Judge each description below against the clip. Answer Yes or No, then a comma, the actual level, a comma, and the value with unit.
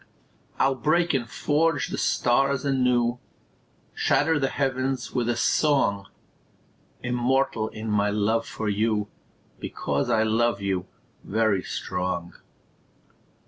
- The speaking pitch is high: No, low, 120 Hz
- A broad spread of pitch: No, average, 4.3 semitones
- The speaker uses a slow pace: Yes, slow, 110 wpm